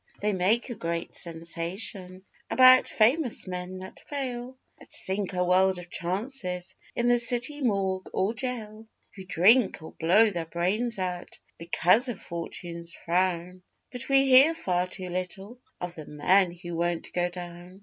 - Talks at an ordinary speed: Yes, average, 155 wpm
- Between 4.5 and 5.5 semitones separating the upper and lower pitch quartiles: Yes, average, 4.8 semitones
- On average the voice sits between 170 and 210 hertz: Yes, medium, 185 Hz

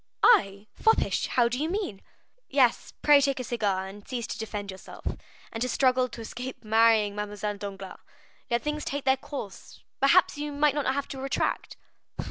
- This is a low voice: No, high, 245 Hz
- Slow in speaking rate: No, average, 175 wpm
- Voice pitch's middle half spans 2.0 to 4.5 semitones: No, average, 5.2 semitones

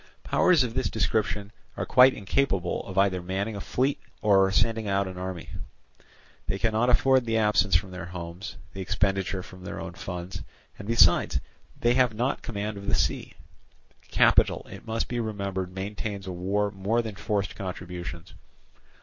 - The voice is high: No, low, 100 Hz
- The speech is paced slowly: No, average, 165 wpm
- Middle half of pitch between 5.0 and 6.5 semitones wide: No, average, 3.2 semitones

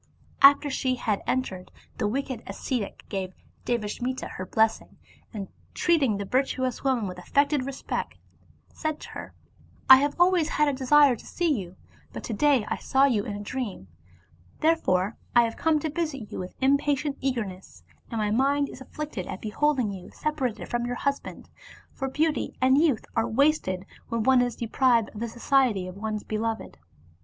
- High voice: Yes, very high, 255 Hz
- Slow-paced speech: No, average, 175 wpm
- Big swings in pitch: No, average, 4.8 semitones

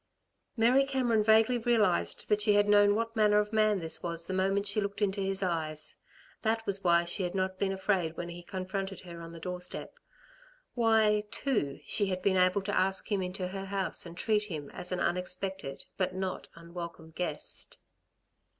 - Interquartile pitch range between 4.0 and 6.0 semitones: No, average, 2.8 semitones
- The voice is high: Yes, high, 195 Hz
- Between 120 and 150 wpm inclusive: No, average, 185 wpm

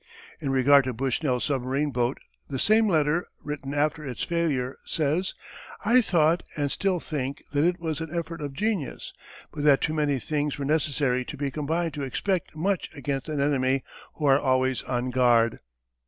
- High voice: No, medium, 145 Hz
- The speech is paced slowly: No, average, 175 wpm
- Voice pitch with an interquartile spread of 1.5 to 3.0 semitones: No, average, 3.4 semitones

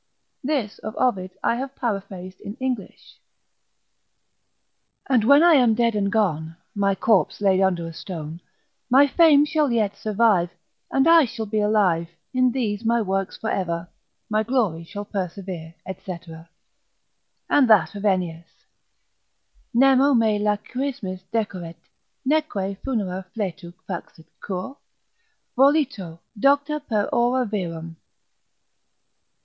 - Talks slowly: Yes, slow, 120 wpm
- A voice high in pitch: Yes, high, 210 Hz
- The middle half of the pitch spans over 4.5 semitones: Yes, wide, 5.4 semitones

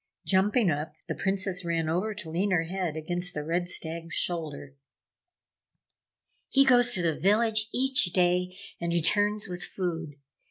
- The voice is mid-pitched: Yes, medium, 180 Hz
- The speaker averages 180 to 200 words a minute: No, average, 150 wpm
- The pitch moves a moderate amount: Yes, average, 3.7 semitones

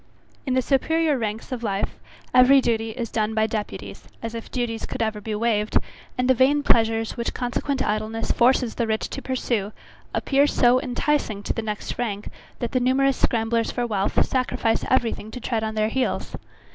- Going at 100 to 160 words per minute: No, average, 185 wpm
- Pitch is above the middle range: Yes, high, 235 Hz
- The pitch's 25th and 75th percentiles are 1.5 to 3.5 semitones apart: Yes, average, 2.7 semitones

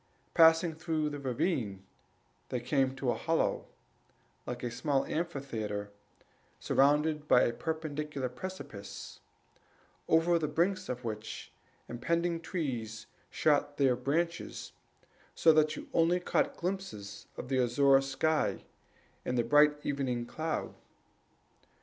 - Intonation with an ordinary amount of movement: Yes, average, 4.7 semitones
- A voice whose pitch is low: No, medium, 145 Hz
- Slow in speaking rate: Yes, slow, 115 wpm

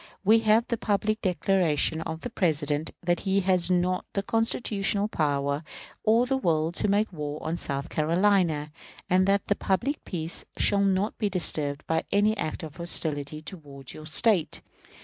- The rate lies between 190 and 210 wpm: No, average, 165 wpm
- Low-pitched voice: No, medium, 180 Hz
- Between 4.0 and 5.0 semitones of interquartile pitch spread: Yes, average, 4.6 semitones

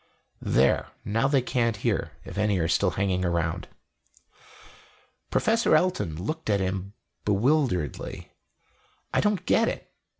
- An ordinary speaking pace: No, slow, 125 wpm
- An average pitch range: No, wide, 7.5 semitones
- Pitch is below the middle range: Yes, low, 105 Hz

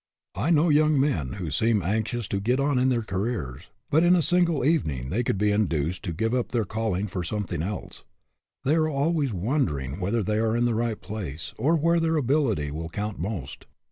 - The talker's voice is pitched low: Yes, low, 110 Hz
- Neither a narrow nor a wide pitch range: No, wide, 7.3 semitones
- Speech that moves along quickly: Yes, fast, 210 wpm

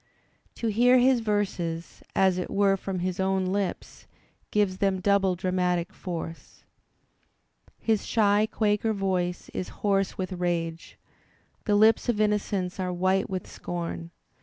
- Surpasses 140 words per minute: No, slow, 135 wpm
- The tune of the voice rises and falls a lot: No, narrow, 2.4 semitones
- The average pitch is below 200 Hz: Yes, high, 190 Hz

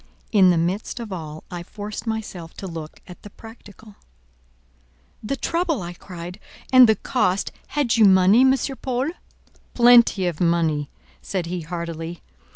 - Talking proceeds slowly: No, average, 150 wpm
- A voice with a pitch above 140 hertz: Yes, high, 190 Hz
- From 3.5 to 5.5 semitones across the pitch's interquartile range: Yes, average, 4.8 semitones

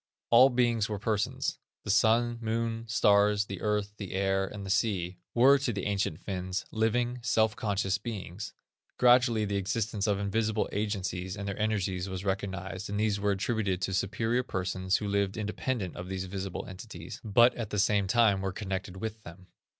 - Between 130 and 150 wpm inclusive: No, average, 175 wpm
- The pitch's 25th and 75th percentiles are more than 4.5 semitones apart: No, narrow, 2.5 semitones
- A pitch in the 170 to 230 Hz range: No, low, 100 Hz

